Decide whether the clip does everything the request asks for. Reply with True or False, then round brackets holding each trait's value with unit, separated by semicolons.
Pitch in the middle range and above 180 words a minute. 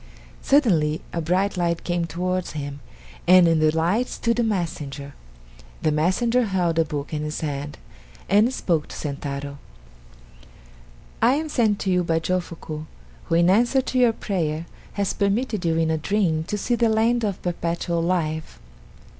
False (175 Hz; 165 wpm)